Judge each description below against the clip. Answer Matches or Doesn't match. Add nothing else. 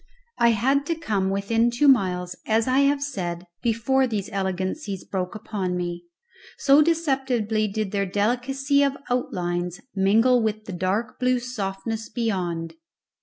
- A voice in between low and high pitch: Doesn't match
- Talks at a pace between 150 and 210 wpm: Doesn't match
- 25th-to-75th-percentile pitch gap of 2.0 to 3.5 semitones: Doesn't match